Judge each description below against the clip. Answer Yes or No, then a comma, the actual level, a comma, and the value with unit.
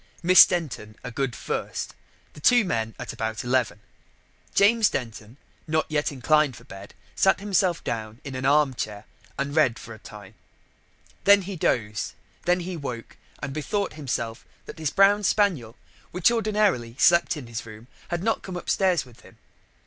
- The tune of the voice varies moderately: No, wide, 7.7 semitones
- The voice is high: No, medium, 140 Hz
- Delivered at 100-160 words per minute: No, average, 170 wpm